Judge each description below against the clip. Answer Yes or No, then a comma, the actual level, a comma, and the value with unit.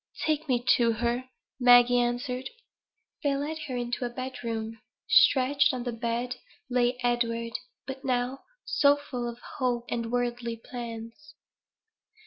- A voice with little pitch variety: Yes, narrow, 1.6 semitones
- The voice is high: Yes, high, 245 Hz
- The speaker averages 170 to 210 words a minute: No, slow, 135 wpm